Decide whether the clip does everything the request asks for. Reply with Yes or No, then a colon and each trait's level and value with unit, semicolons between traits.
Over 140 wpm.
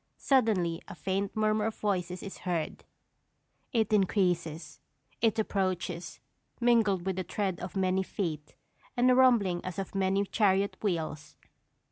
No: slow, 135 wpm